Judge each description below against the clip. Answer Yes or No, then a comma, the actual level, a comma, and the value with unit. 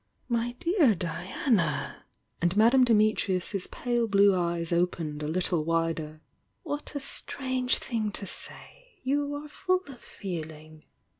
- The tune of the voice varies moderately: No, wide, 7.4 semitones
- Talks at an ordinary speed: No, slow, 130 wpm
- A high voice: Yes, high, 205 Hz